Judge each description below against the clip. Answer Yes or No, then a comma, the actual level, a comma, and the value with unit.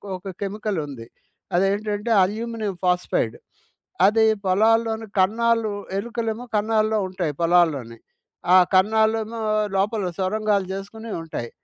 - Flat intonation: No, average, 3.1 semitones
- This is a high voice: Yes, high, 210 Hz